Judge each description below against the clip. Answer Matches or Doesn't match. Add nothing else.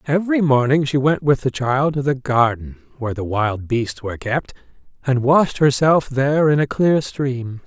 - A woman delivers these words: Doesn't match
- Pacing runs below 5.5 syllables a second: Matches